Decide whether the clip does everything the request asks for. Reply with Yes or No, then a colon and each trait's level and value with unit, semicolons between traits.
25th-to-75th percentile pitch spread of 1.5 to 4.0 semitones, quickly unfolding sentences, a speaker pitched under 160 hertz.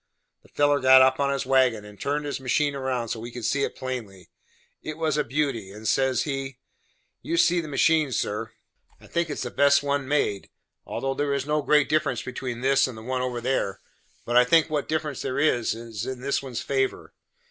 Yes: average, 3.0 semitones; fast, 215 wpm; low, 135 Hz